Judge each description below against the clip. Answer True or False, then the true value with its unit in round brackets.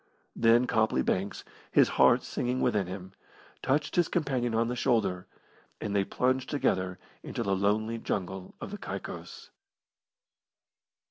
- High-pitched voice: False (110 Hz)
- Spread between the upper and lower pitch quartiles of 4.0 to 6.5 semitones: True (4.7 semitones)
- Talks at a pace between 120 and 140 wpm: True (135 wpm)